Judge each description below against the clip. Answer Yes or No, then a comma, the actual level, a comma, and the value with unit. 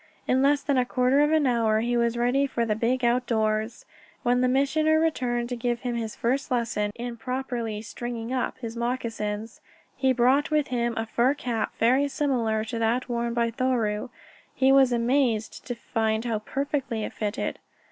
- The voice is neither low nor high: No, high, 240 Hz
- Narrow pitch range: Yes, narrow, 2.3 semitones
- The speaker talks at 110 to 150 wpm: No, average, 180 wpm